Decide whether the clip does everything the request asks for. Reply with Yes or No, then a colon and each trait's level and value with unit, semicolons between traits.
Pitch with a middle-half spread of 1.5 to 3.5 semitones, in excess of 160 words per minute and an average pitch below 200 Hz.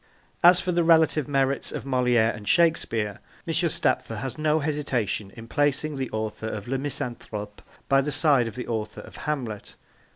No: average, 5.1 semitones; average, 170 wpm; low, 135 Hz